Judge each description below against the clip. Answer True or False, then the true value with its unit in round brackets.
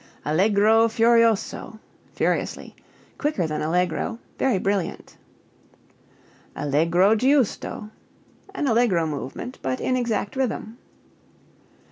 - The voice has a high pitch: True (215 Hz)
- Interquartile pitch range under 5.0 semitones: False (5.4 semitones)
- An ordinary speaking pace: False (85 wpm)